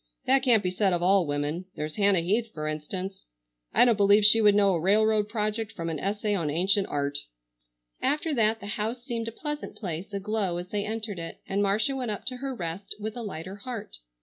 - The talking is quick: Yes, fast, 215 wpm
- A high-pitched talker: Yes, high, 205 Hz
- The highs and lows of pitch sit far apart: No, average, 3.6 semitones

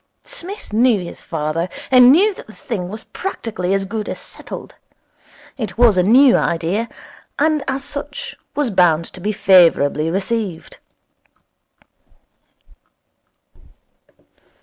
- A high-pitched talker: Yes, high, 215 Hz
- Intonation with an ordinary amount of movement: No, wide, 6.2 semitones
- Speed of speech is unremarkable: No, slow, 125 wpm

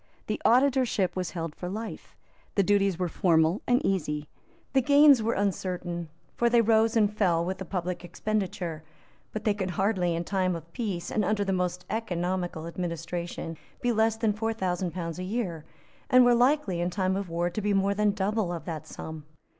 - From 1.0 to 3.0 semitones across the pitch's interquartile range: No, average, 3.9 semitones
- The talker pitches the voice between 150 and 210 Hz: Yes, high, 190 Hz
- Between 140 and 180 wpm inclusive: No, average, 190 wpm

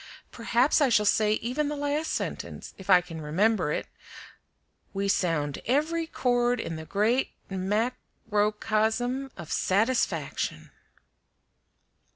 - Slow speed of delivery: Yes, slow, 125 wpm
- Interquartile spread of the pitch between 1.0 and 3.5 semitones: No, average, 4.8 semitones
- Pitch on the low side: No, high, 220 Hz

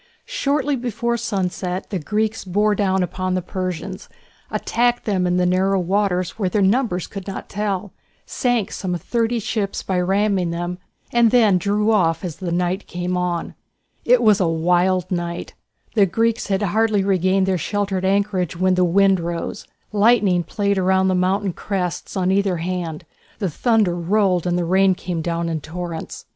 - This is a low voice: No, high, 190 Hz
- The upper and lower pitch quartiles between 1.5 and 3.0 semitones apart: Yes, narrow, 2.5 semitones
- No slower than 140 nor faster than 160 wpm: No, average, 170 wpm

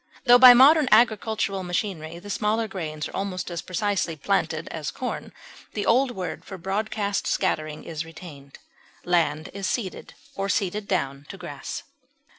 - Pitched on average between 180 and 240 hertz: Yes, high, 190 Hz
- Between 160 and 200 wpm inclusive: No, average, 150 wpm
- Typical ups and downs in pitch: Yes, average, 4.7 semitones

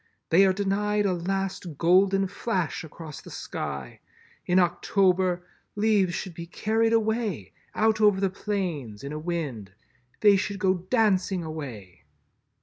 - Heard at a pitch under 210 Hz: Yes, medium, 185 Hz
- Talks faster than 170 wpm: No, average, 140 wpm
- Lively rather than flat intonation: No, average, 3.6 semitones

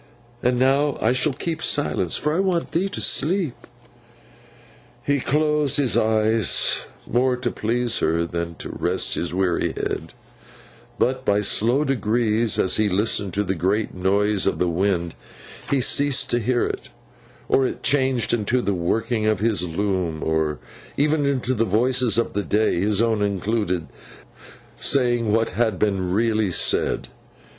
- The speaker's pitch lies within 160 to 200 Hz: No, low, 110 Hz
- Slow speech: No, average, 155 wpm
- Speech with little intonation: No, average, 4.8 semitones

